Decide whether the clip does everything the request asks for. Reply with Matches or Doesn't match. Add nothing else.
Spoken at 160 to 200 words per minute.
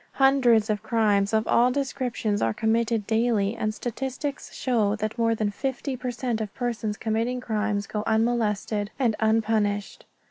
Doesn't match